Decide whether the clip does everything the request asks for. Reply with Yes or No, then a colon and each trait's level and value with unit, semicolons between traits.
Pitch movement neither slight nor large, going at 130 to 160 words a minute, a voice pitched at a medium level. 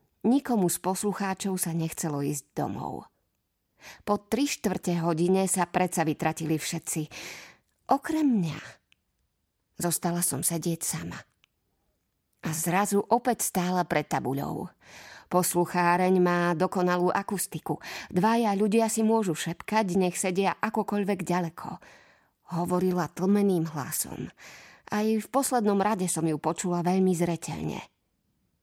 No: average, 3.6 semitones; slow, 110 wpm; medium, 180 Hz